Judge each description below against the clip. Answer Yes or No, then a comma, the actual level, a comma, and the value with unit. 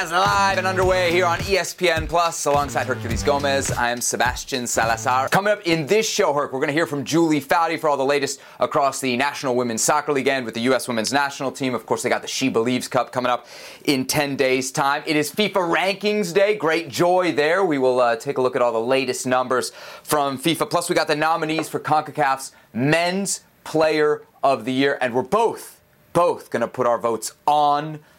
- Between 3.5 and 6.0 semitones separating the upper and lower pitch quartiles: Yes, average, 4.2 semitones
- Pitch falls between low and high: Yes, medium, 145 Hz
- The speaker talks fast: Yes, fast, 215 wpm